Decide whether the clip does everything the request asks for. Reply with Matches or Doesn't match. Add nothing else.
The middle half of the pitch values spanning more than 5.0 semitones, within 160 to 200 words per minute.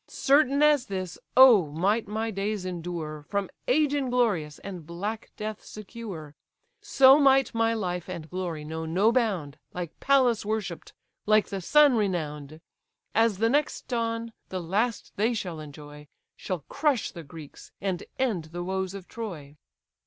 Doesn't match